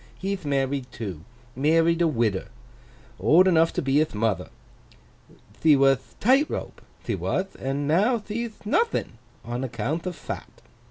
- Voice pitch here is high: No, medium, 155 Hz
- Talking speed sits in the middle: No, slow, 130 wpm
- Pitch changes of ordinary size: No, wide, 6.2 semitones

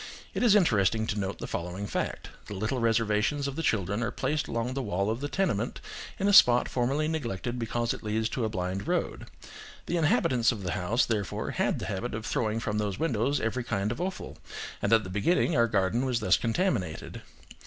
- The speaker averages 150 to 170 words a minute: No, fast, 205 wpm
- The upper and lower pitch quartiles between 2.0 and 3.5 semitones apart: No, average, 4.2 semitones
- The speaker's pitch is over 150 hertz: No, low, 115 Hz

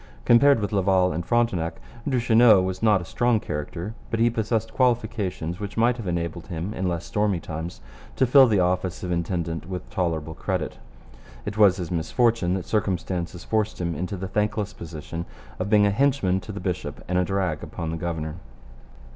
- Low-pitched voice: Yes, very low, 95 Hz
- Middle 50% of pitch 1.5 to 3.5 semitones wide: No, average, 4.2 semitones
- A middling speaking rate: Yes, average, 180 wpm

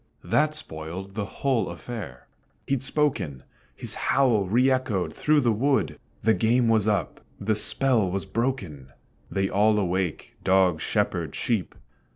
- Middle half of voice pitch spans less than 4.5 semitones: No, average, 5.3 semitones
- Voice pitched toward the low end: Yes, low, 110 Hz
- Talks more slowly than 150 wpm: Yes, average, 140 wpm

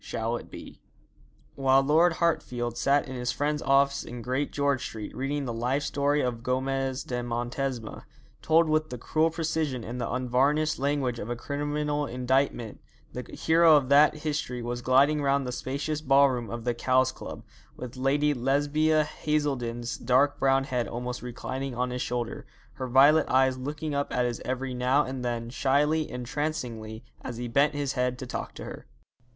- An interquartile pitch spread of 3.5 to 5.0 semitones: No, average, 2.9 semitones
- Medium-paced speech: Yes, average, 175 wpm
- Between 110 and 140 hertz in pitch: Yes, low, 135 Hz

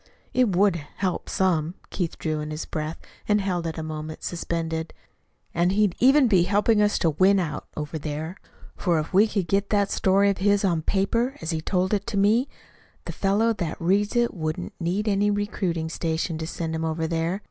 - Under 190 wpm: No, average, 200 wpm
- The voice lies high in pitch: No, medium, 180 Hz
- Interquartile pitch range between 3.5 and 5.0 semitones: Yes, average, 4.0 semitones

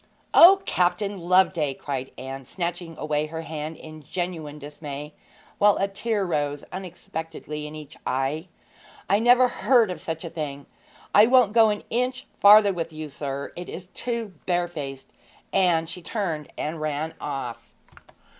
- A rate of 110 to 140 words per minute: No, average, 150 wpm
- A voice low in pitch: No, medium, 165 Hz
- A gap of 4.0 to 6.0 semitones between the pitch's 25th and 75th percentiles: Yes, average, 4.7 semitones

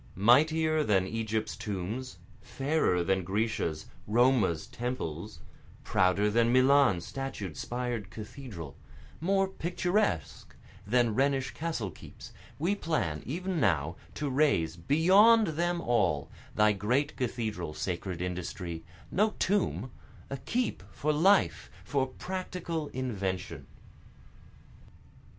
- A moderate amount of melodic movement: No, wide, 8.5 semitones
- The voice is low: Yes, low, 120 Hz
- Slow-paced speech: Yes, slow, 105 wpm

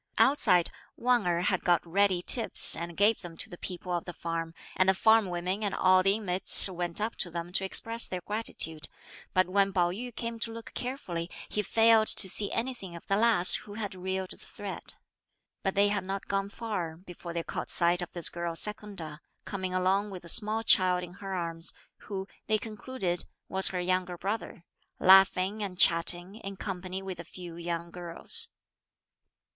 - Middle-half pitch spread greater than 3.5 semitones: No, average, 3.0 semitones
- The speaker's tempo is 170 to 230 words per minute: Yes, average, 190 wpm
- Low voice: No, medium, 185 Hz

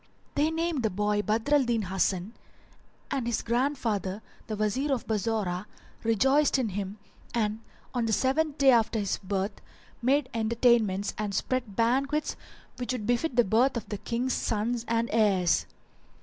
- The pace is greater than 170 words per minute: No, average, 150 wpm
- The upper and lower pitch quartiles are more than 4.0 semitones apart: No, average, 3.7 semitones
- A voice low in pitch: No, high, 230 Hz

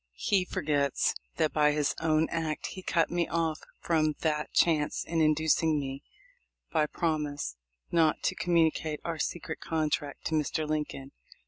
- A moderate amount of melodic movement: No, narrow, 1.6 semitones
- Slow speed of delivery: No, average, 150 wpm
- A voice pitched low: No, medium, 155 Hz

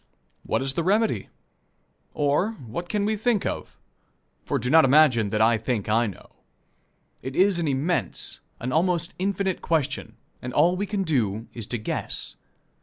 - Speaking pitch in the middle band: Yes, medium, 155 Hz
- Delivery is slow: No, average, 165 wpm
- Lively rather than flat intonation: Yes, wide, 7.6 semitones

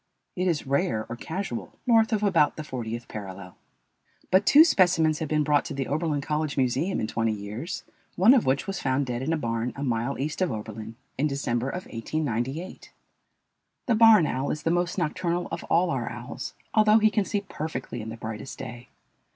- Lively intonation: Yes, wide, 6.9 semitones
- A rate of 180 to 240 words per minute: Yes, average, 195 wpm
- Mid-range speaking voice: Yes, medium, 150 Hz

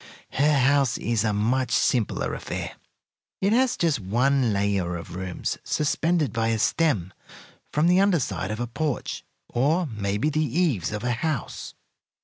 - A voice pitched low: Yes, low, 125 Hz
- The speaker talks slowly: No, average, 155 wpm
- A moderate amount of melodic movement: No, wide, 6.6 semitones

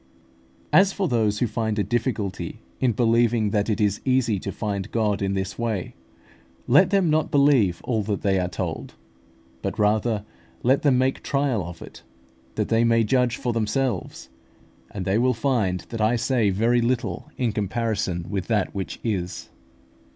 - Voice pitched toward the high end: No, low, 110 Hz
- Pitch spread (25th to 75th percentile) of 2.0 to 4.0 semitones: Yes, average, 3.4 semitones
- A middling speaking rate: Yes, average, 170 wpm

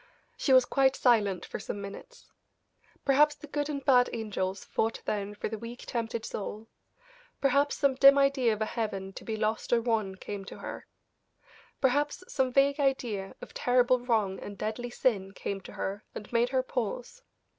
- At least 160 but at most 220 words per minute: Yes, average, 175 wpm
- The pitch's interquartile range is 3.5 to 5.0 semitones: Yes, average, 4.4 semitones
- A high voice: Yes, high, 240 Hz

